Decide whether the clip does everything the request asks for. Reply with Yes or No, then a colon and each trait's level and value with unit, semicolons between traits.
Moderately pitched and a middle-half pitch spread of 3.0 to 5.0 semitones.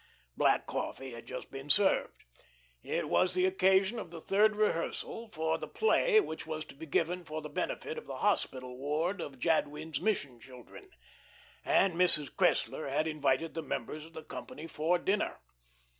Yes: medium, 160 Hz; average, 4.2 semitones